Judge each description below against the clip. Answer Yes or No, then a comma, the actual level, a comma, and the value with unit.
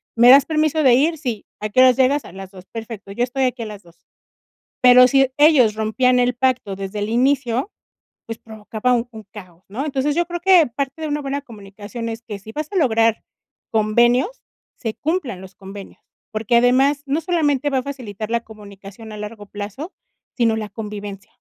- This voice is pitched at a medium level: No, high, 240 Hz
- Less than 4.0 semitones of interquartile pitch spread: No, average, 4.5 semitones